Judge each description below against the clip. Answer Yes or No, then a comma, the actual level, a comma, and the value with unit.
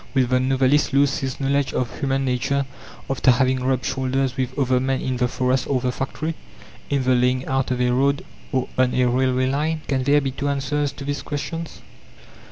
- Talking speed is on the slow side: No, average, 200 wpm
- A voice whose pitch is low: Yes, low, 130 Hz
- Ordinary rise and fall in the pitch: No, narrow, 1.5 semitones